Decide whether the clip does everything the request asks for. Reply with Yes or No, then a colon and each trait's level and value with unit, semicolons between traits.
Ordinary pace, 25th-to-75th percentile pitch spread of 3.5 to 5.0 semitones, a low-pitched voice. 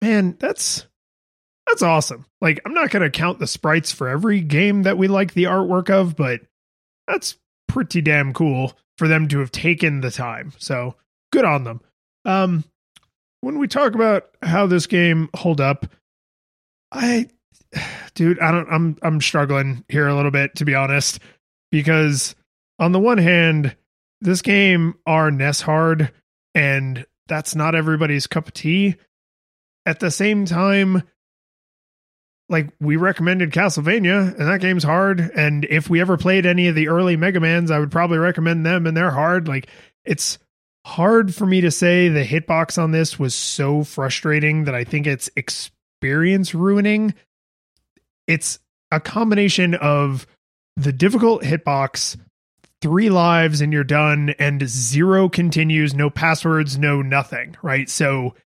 No: average, 155 wpm; average, 4.0 semitones; medium, 160 Hz